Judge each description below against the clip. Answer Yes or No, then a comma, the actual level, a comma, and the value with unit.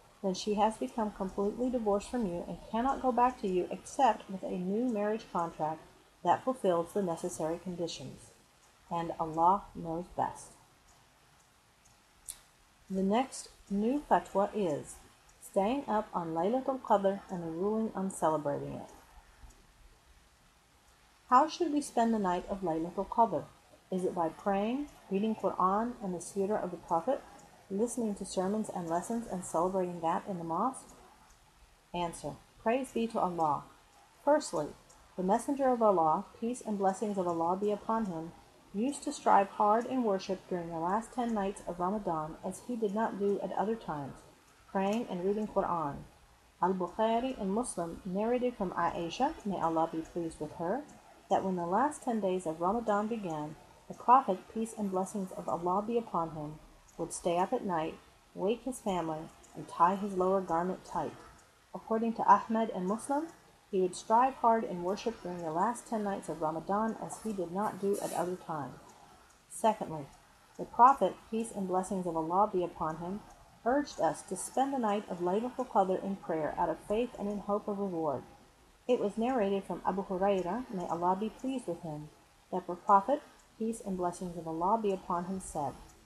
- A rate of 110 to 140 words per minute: No, average, 170 wpm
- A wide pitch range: No, average, 4.3 semitones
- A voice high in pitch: Yes, high, 195 Hz